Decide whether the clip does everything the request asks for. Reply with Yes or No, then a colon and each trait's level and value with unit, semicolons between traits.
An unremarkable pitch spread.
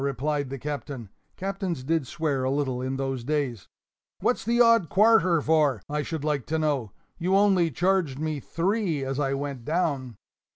Yes: average, 4.3 semitones